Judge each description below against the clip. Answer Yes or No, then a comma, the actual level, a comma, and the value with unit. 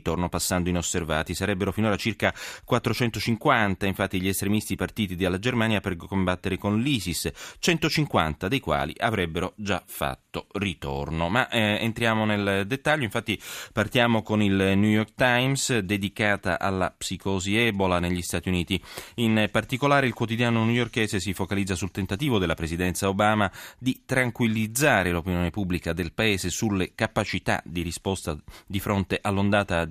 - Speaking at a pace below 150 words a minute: Yes, average, 140 wpm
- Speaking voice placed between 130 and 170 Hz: No, low, 100 Hz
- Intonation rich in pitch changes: No, average, 3.6 semitones